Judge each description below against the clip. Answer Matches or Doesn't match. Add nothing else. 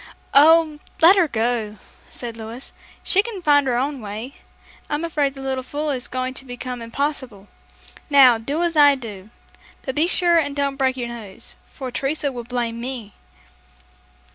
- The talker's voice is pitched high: Matches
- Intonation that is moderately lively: Matches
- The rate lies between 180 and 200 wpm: Doesn't match